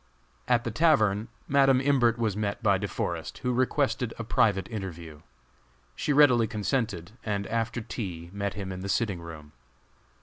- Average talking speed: Yes, average, 160 wpm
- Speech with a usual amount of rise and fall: Yes, average, 4.1 semitones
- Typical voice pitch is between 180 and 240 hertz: No, low, 110 Hz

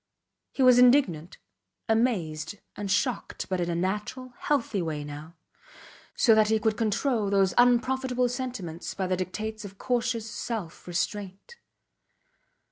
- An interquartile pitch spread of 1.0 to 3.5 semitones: No, average, 5.0 semitones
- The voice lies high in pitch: Yes, high, 215 Hz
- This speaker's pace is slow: Yes, slow, 130 wpm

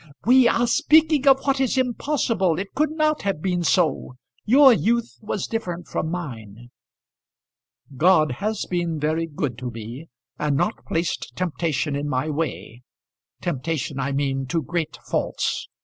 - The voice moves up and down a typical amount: No, wide, 8.2 semitones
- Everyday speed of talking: Yes, average, 150 wpm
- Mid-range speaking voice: Yes, medium, 170 Hz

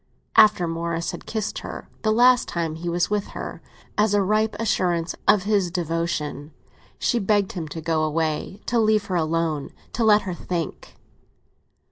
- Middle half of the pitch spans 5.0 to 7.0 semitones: No, average, 4.3 semitones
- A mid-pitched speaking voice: Yes, medium, 180 Hz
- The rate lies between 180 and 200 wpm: No, average, 165 wpm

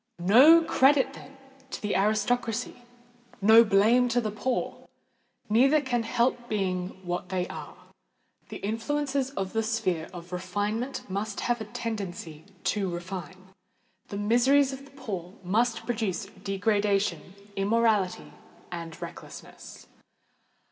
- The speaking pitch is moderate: No, high, 220 Hz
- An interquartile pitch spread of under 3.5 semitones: No, average, 4.2 semitones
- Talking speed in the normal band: No, slow, 120 wpm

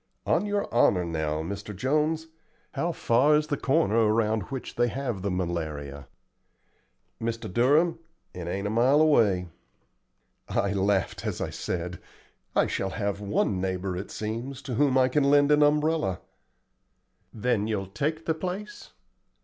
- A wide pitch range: Yes, wide, 7.3 semitones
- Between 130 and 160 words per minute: Yes, average, 150 wpm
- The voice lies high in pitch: No, low, 115 Hz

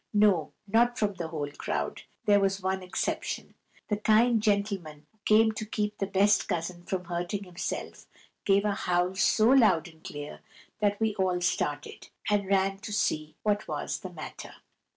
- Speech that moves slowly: No, average, 170 wpm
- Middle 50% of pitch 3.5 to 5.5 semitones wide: No, average, 3.0 semitones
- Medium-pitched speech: No, high, 195 Hz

